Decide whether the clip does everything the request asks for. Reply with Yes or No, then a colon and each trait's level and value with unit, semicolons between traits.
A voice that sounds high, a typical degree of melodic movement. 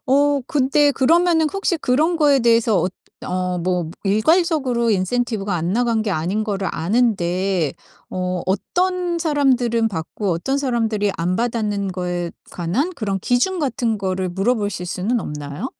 No: high, 220 Hz; wide, 6.6 semitones